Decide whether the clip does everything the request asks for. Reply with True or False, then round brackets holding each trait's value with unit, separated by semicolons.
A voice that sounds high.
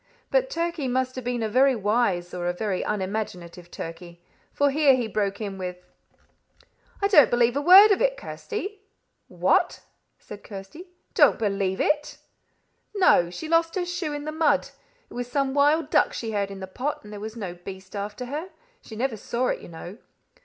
True (240 Hz)